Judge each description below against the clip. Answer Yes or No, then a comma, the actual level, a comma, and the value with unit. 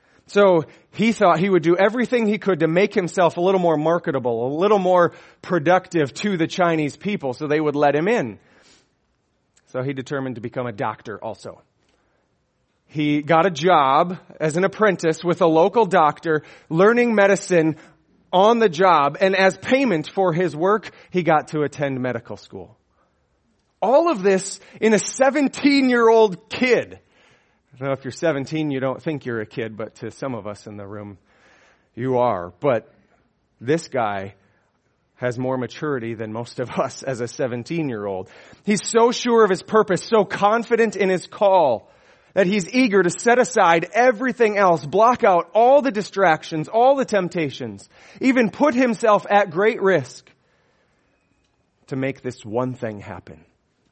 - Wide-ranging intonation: Yes, wide, 7.3 semitones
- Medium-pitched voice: Yes, medium, 170 Hz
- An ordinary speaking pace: Yes, average, 165 wpm